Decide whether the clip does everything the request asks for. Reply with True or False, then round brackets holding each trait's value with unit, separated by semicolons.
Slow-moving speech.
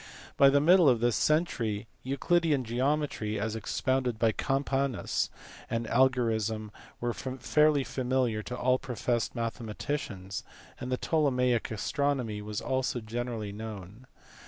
True (125 wpm)